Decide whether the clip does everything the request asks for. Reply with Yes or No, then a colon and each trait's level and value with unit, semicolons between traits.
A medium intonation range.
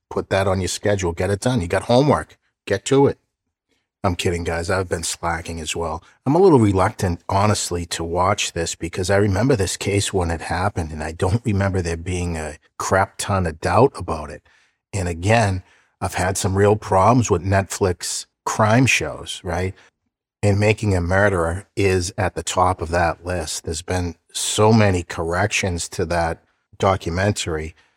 Yes: average, 3.0 semitones